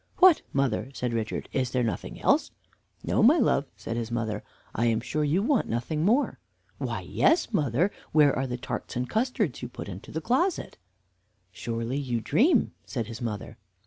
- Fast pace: No, average, 175 wpm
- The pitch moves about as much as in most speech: No, wide, 8.1 semitones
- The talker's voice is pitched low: Yes, low, 125 Hz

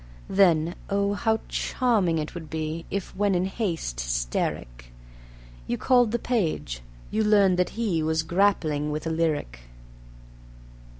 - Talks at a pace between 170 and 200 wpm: No, slow, 135 wpm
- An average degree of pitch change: Yes, average, 4.7 semitones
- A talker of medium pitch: Yes, medium, 170 Hz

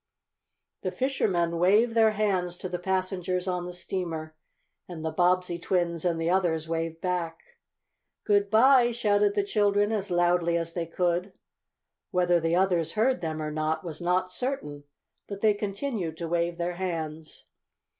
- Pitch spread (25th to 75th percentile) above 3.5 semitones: No, average, 3.2 semitones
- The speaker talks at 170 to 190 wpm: No, average, 155 wpm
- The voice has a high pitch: No, medium, 180 Hz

